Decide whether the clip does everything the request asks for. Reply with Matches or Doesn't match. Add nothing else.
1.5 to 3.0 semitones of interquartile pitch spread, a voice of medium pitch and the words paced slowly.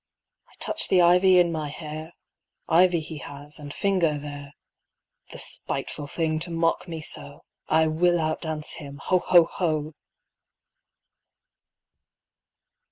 Matches